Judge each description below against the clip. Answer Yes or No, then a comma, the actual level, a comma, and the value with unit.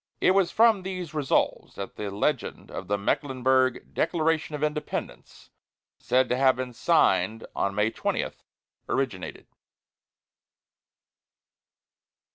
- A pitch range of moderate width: No, wide, 5.7 semitones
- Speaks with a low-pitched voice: Yes, low, 130 Hz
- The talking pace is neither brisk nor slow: No, slow, 105 wpm